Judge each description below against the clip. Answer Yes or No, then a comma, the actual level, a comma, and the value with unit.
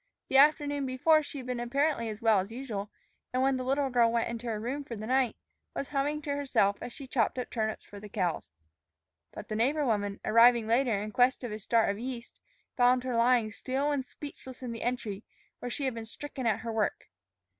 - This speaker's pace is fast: Yes, fast, 220 wpm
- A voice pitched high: Yes, high, 245 Hz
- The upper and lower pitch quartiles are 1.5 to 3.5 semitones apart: Yes, average, 3.2 semitones